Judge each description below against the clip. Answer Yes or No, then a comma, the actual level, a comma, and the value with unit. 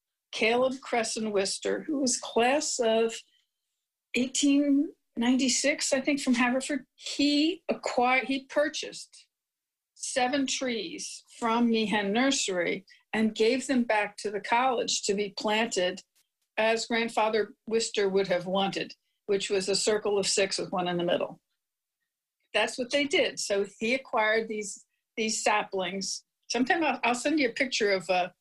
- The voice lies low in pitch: No, high, 230 Hz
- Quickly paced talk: No, average, 140 wpm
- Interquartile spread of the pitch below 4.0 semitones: No, average, 4.4 semitones